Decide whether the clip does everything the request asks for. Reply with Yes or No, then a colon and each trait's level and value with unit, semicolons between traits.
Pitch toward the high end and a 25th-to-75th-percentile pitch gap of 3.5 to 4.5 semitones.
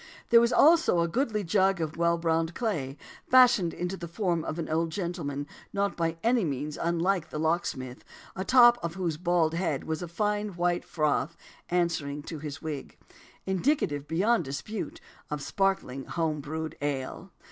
No: medium, 170 Hz; average, 3.9 semitones